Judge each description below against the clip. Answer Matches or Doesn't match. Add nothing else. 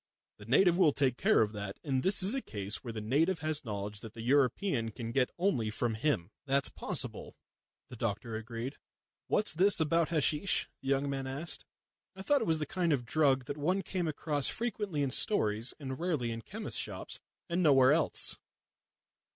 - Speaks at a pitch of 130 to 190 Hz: Matches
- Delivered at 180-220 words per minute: Matches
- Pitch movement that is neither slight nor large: Doesn't match